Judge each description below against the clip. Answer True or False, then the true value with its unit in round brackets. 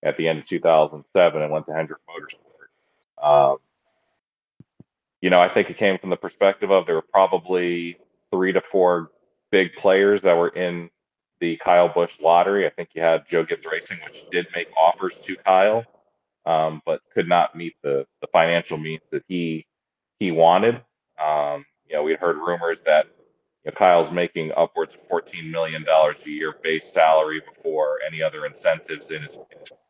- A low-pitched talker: True (85 Hz)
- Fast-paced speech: False (175 wpm)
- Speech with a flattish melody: False (3.9 semitones)